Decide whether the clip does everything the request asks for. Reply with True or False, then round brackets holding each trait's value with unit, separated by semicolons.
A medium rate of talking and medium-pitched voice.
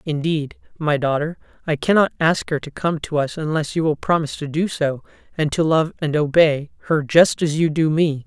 False (210 wpm; 155 Hz)